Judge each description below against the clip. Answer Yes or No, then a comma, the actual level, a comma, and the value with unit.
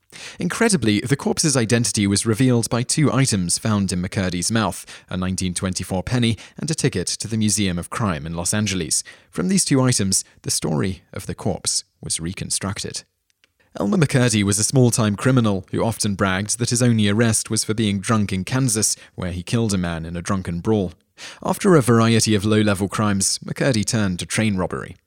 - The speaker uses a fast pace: No, average, 190 wpm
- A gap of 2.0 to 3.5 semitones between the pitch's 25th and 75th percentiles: No, average, 4.4 semitones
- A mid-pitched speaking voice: No, low, 105 Hz